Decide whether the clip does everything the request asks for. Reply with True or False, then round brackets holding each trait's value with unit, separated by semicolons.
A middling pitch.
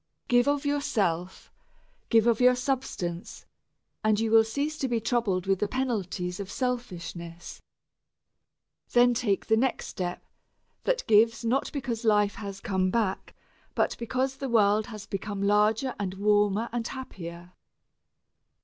False (220 Hz)